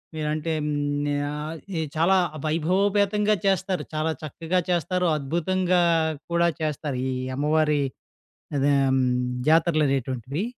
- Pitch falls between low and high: Yes, medium, 160 Hz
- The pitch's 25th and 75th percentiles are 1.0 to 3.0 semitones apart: No, average, 3.5 semitones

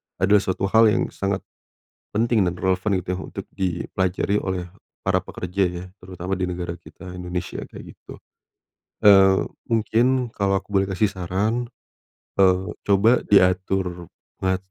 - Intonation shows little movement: Yes, narrow, 2.1 semitones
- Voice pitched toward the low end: Yes, very low, 95 Hz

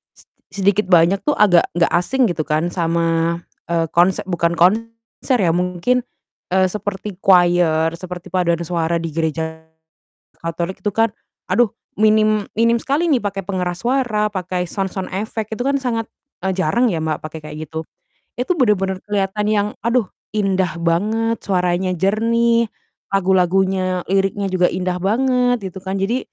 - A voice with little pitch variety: No, average, 3.7 semitones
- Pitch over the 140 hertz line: Yes, high, 190 Hz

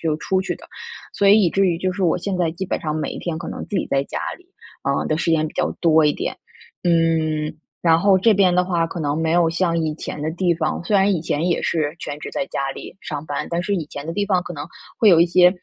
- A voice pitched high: No, medium, 170 Hz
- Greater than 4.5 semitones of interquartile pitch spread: No, average, 2.8 semitones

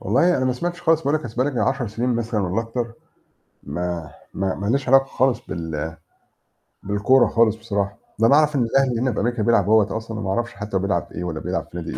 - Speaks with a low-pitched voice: Yes, low, 115 Hz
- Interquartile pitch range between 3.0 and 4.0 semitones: No, average, 4.9 semitones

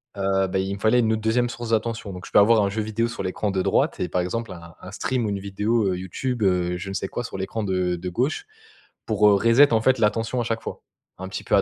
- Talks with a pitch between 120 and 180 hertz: No, low, 105 Hz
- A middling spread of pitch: Yes, average, 3.3 semitones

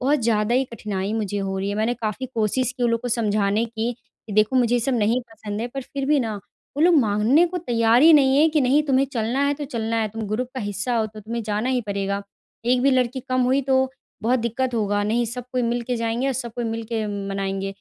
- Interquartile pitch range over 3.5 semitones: No, average, 3.2 semitones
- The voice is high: Yes, high, 230 Hz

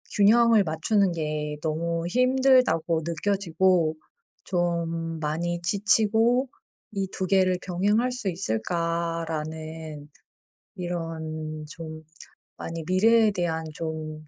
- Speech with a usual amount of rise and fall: Yes, average, 3.8 semitones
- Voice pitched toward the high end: No, medium, 170 Hz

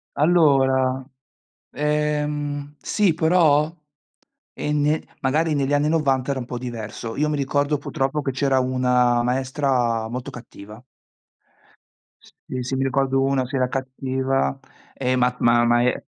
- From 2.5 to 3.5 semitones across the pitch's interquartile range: Yes, average, 2.8 semitones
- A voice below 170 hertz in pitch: Yes, low, 135 Hz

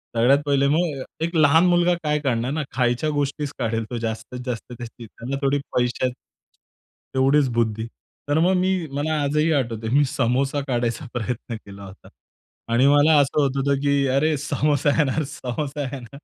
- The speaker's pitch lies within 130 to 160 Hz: Yes, medium, 140 Hz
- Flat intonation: No, average, 3.5 semitones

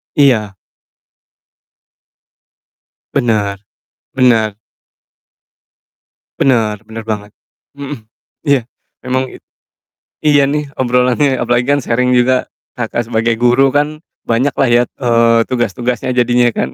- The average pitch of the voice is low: Yes, low, 125 Hz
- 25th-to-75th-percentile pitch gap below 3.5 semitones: Yes, average, 2.7 semitones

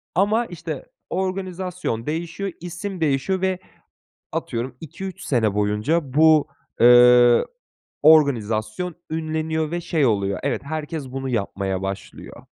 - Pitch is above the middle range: No, medium, 155 Hz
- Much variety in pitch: Yes, wide, 6.4 semitones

